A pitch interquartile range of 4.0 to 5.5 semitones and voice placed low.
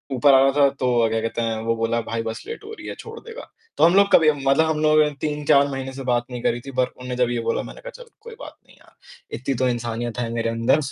Yes: average, 4.5 semitones; low, 130 Hz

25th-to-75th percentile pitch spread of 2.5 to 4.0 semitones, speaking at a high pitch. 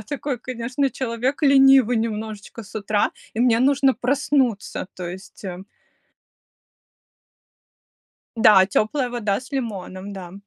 No: average, 4.4 semitones; high, 230 Hz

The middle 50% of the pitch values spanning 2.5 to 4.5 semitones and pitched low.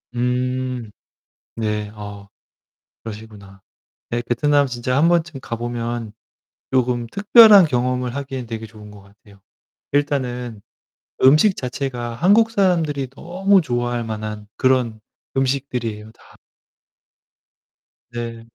Yes: average, 3.8 semitones; low, 125 Hz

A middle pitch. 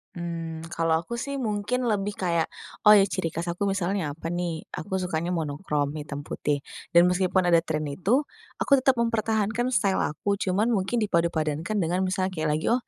Yes: medium, 180 Hz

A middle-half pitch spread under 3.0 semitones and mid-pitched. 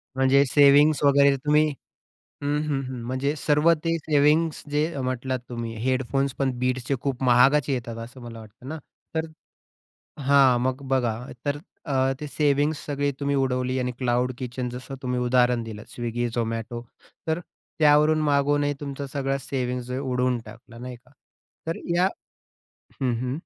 No: narrow, 2.6 semitones; low, 130 Hz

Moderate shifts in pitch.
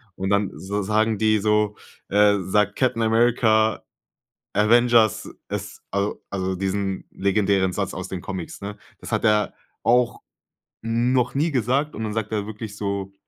No: narrow, 2.3 semitones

